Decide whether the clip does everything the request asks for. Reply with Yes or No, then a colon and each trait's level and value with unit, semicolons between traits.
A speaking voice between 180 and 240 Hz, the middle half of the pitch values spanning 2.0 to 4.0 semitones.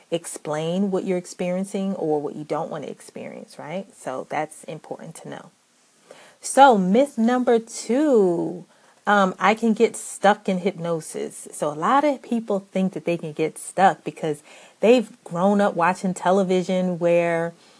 No: high, 190 Hz; average, 4.4 semitones